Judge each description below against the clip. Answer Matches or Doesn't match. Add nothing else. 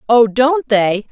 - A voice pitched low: Doesn't match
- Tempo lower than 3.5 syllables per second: Matches